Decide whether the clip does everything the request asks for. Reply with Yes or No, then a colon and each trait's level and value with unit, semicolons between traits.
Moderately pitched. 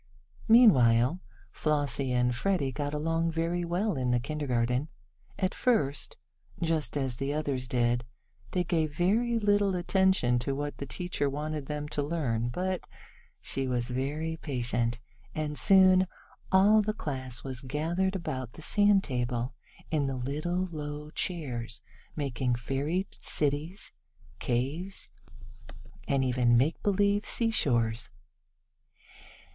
Yes: medium, 145 Hz